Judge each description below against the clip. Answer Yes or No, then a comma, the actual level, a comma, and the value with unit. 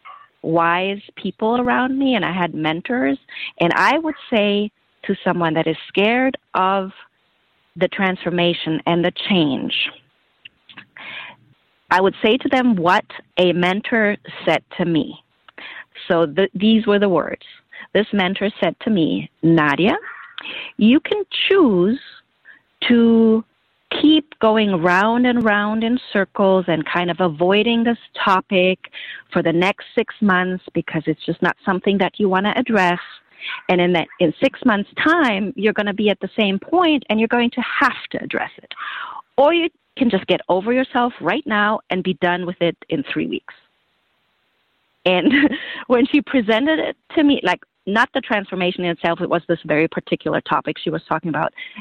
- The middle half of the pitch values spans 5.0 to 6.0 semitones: Yes, wide, 5.5 semitones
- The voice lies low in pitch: No, high, 205 Hz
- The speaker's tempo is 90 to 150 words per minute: No, average, 165 wpm